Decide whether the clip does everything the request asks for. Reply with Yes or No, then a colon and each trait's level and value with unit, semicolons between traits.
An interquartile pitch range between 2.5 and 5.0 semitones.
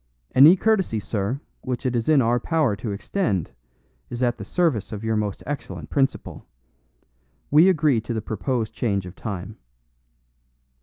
No: wide, 5.6 semitones